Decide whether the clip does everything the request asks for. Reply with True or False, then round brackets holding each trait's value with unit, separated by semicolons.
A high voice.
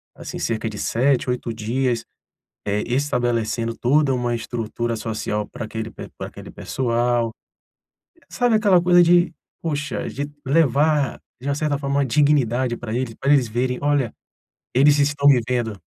False (125 Hz)